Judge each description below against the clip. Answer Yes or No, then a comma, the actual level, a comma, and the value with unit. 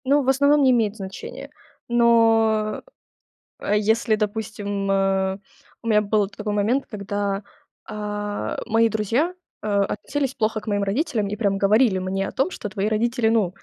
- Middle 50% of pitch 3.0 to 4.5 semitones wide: No, narrow, 2.4 semitones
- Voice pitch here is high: Yes, high, 215 Hz